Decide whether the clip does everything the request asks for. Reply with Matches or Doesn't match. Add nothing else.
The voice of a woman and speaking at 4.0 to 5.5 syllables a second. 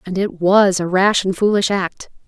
Matches